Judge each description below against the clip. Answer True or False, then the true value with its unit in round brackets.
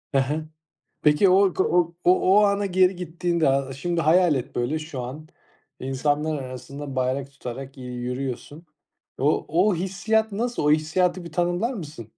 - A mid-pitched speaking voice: True (155 Hz)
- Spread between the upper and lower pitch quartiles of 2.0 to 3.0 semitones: False (5.0 semitones)